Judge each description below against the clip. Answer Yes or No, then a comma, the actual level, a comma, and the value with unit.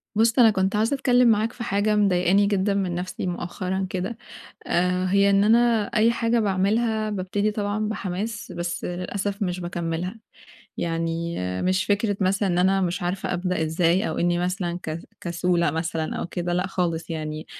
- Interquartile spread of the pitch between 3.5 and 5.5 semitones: No, average, 3.1 semitones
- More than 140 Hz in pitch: Yes, high, 190 Hz